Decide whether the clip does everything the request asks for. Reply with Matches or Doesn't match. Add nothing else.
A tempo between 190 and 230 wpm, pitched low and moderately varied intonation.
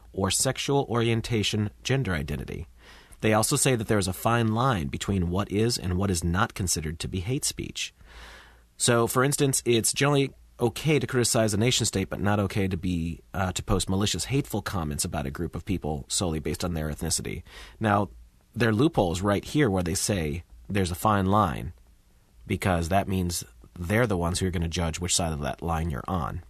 Matches